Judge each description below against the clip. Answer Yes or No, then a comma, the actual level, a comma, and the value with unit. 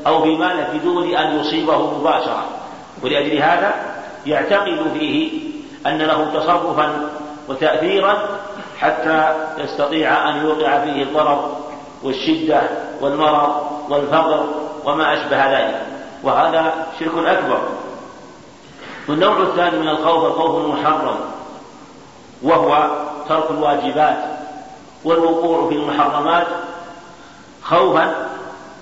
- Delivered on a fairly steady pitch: Yes, narrow, 2.3 semitones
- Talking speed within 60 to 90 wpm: Yes, average, 85 wpm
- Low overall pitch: No, medium, 155 Hz